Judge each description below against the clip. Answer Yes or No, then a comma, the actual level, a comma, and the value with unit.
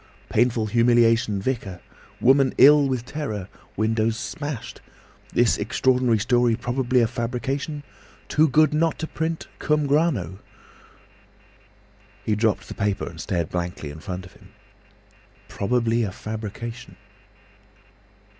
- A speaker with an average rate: No, slow, 110 wpm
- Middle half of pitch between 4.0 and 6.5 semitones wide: Yes, average, 4.3 semitones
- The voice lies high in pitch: No, low, 120 Hz